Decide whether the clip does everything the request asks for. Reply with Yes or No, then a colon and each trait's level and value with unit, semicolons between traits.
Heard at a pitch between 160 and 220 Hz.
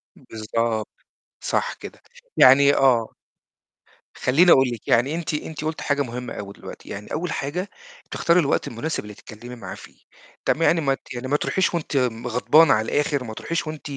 No: low, 135 Hz